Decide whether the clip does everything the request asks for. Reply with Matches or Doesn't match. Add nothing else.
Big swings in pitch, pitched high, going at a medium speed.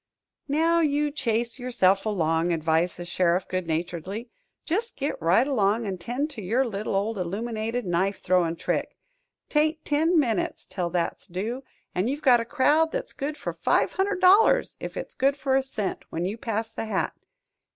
Matches